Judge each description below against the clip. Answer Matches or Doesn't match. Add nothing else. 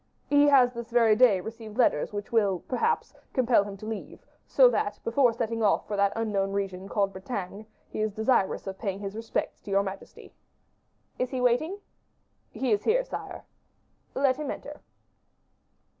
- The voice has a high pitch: Matches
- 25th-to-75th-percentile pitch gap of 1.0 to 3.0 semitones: Doesn't match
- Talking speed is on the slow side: Doesn't match